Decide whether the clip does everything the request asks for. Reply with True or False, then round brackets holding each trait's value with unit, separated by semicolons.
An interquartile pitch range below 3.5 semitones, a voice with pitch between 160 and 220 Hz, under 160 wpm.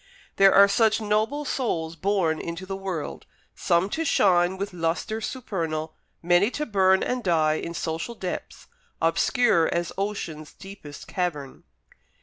False (4.1 semitones; 185 Hz; 135 wpm)